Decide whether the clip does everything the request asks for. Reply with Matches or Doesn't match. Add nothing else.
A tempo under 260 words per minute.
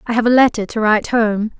Doesn't match